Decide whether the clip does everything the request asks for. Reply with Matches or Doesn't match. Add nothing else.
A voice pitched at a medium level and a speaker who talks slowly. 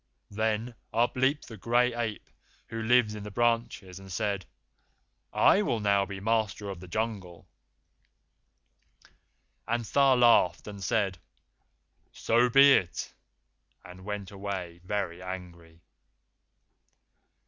Doesn't match